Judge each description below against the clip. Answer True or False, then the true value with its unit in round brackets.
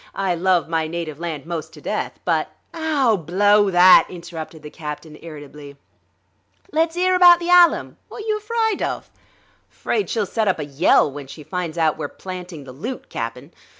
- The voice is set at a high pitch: False (175 Hz)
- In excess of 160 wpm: True (180 wpm)